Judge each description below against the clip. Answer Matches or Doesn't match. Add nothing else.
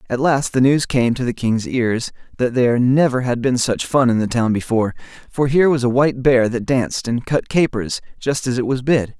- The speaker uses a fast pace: Matches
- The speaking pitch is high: Doesn't match